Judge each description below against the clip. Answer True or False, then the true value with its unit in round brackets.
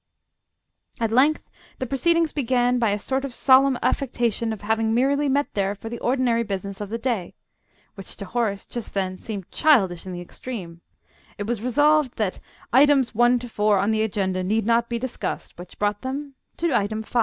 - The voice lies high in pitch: True (230 Hz)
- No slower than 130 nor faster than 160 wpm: False (190 wpm)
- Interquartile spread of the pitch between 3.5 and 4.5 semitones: True (4.2 semitones)